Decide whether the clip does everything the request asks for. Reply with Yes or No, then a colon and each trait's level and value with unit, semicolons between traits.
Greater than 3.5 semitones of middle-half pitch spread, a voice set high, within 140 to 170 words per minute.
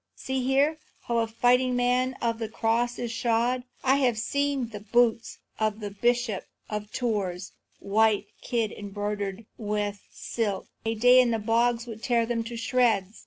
No: narrow, 2.5 semitones; high, 230 Hz; average, 165 wpm